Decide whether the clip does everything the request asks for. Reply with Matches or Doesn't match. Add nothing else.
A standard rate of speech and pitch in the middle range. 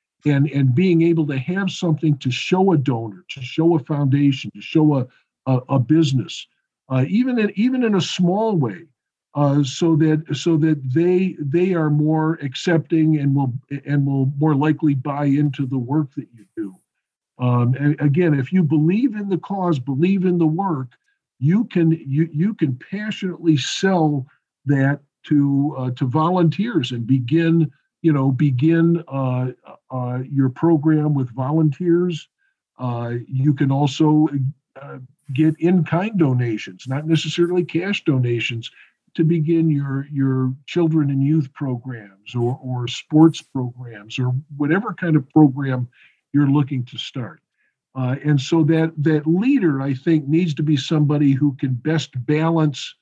Matches